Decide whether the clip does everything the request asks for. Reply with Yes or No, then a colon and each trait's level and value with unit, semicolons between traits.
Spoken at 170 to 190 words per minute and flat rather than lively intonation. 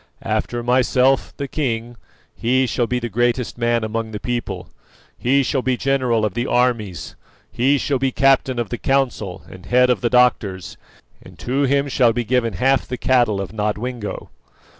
Yes: average, 175 wpm; narrow, 2.3 semitones